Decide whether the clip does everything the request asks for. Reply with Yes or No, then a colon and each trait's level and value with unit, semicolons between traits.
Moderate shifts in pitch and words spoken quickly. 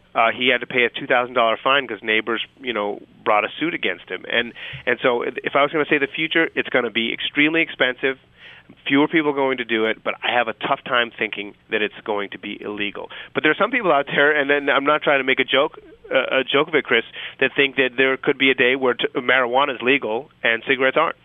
Yes: average, 4.0 semitones; fast, 260 wpm